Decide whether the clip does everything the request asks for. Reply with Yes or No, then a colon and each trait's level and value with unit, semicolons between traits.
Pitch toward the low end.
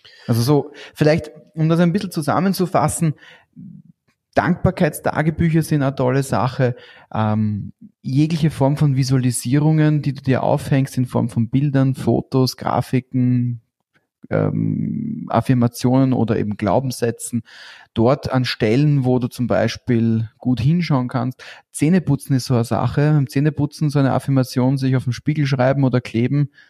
Yes: low, 130 Hz